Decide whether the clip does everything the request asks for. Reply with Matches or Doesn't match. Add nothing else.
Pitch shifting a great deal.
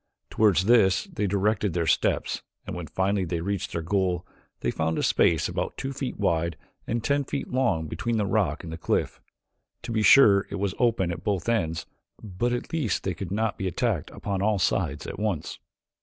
Doesn't match